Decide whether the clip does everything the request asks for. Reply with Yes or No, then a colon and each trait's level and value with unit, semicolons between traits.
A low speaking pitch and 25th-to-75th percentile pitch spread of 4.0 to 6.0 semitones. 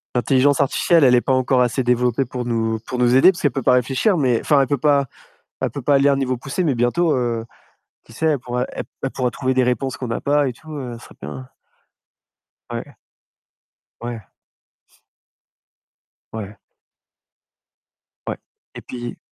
No: low, 130 Hz; narrow, 2.6 semitones